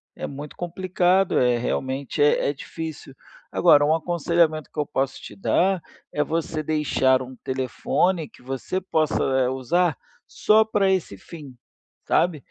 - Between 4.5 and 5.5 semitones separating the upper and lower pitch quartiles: Yes, average, 4.8 semitones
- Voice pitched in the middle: Yes, medium, 155 Hz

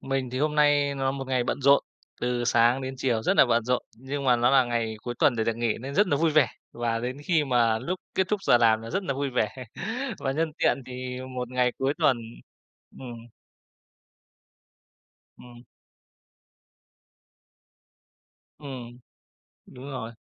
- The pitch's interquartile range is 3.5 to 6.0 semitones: No, narrow, 2.6 semitones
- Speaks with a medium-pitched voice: No, low, 130 Hz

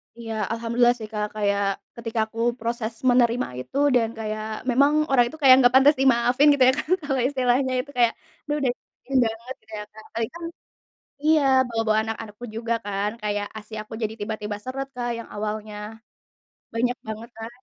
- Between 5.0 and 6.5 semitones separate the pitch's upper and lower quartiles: No, average, 2.9 semitones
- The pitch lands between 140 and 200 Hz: No, high, 230 Hz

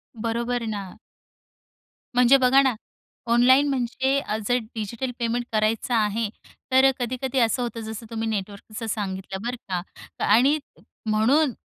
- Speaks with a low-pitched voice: No, high, 235 Hz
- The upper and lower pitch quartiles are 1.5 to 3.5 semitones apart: Yes, average, 2.9 semitones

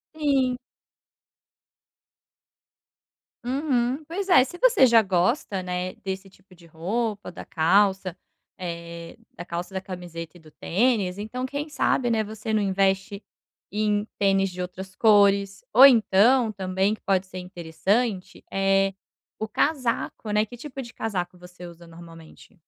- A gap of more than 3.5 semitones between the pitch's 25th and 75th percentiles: Yes, average, 4.5 semitones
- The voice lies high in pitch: Yes, high, 195 Hz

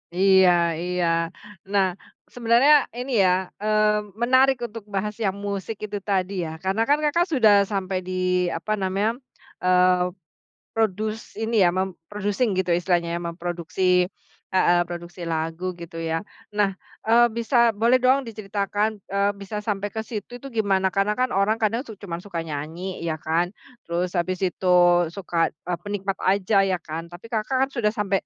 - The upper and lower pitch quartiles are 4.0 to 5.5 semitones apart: No, average, 3.3 semitones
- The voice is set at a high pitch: Yes, high, 195 Hz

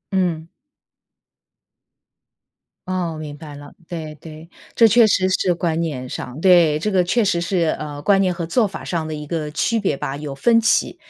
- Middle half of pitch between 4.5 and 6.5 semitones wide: No, average, 3.6 semitones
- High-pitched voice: No, medium, 170 Hz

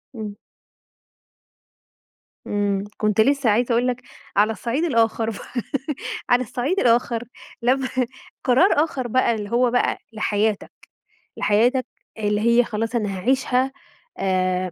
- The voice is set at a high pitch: Yes, high, 235 Hz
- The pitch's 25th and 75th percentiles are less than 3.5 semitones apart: Yes, average, 3.1 semitones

